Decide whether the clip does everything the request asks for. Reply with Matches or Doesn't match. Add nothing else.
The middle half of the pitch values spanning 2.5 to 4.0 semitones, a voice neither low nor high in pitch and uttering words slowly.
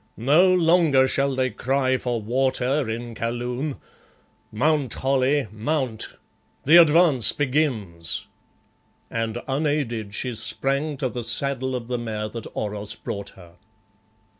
Doesn't match